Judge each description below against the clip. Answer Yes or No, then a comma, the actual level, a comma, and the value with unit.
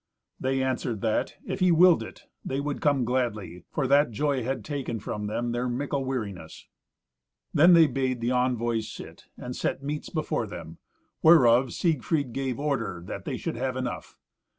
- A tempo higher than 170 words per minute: No, average, 165 wpm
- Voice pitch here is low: Yes, low, 130 Hz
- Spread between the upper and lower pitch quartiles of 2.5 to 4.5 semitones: Yes, average, 3.7 semitones